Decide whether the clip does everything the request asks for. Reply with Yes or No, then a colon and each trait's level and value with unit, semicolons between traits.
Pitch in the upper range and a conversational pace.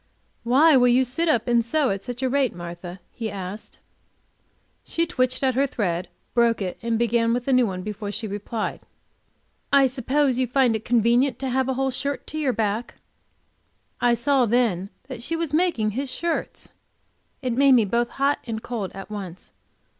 Yes: high, 240 Hz; average, 185 wpm